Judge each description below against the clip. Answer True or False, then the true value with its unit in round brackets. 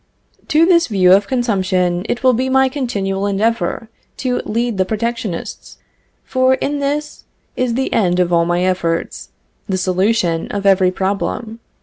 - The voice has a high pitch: True (210 Hz)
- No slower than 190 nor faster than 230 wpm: False (150 wpm)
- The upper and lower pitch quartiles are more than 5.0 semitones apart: True (5.4 semitones)